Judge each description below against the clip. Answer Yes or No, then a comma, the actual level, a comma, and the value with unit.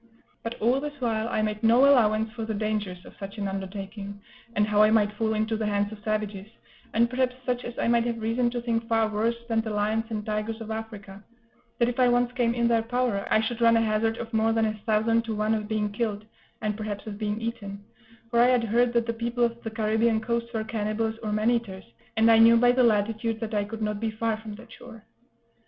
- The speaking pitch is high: Yes, high, 225 Hz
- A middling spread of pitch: No, narrow, 1.6 semitones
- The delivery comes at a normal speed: No, fast, 240 wpm